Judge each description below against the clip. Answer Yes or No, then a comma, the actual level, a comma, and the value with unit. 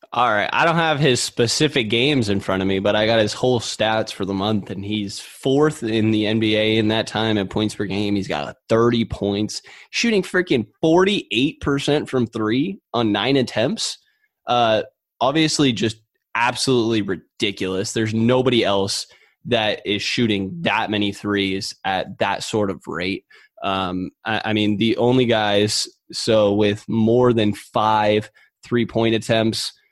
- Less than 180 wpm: Yes, average, 160 wpm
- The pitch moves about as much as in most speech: Yes, average, 3.2 semitones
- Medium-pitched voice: No, low, 110 Hz